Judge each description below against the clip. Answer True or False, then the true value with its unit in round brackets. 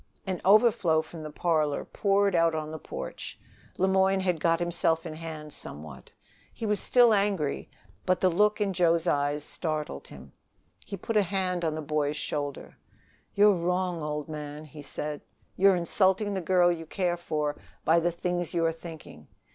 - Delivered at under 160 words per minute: False (175 wpm)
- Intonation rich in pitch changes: False (3.7 semitones)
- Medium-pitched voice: True (170 Hz)